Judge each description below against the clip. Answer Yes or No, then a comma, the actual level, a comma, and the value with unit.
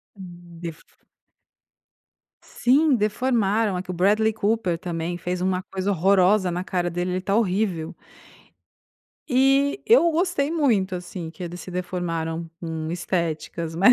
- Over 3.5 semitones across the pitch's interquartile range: Yes, average, 4.0 semitones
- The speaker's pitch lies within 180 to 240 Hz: Yes, medium, 185 Hz